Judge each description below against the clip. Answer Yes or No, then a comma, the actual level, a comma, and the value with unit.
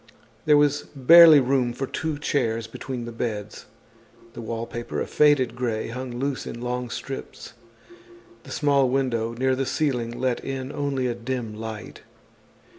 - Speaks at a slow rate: No, average, 150 wpm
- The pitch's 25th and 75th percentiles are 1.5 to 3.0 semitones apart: Yes, average, 2.7 semitones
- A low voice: Yes, low, 125 Hz